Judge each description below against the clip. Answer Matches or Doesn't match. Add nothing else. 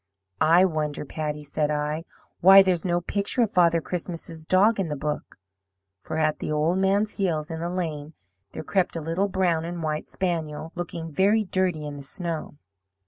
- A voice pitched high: Doesn't match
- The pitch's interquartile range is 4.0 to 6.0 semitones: Doesn't match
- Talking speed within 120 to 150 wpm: Doesn't match